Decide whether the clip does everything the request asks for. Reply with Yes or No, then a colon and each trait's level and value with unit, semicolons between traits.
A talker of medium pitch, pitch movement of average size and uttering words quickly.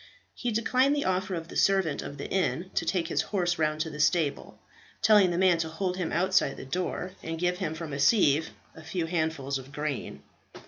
Yes: medium, 170 Hz; average, 3.3 semitones; fast, 215 wpm